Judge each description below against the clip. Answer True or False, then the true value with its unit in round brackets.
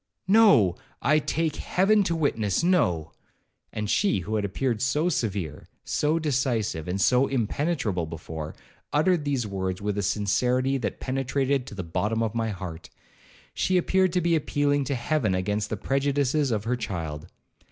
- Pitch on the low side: True (125 Hz)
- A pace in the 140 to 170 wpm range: True (150 wpm)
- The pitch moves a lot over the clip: True (6.7 semitones)